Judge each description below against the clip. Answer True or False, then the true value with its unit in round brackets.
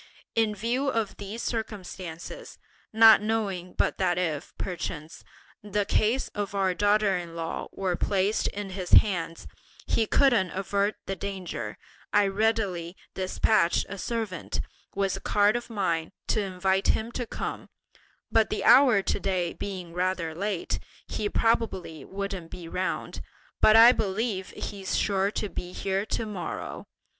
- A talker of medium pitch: False (195 Hz)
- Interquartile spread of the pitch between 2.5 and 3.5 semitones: True (2.9 semitones)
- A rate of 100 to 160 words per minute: True (145 wpm)